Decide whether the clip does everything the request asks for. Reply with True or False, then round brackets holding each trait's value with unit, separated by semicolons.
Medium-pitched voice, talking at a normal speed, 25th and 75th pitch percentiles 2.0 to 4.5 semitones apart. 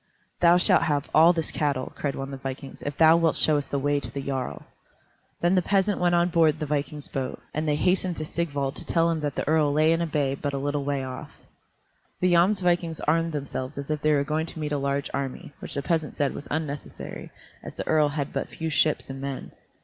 False (150 Hz; 240 wpm; 2.8 semitones)